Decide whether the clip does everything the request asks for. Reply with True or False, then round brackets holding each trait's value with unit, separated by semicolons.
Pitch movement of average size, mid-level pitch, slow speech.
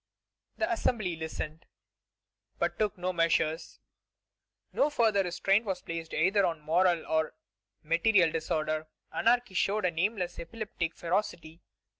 True (4.2 semitones; 180 Hz; 125 wpm)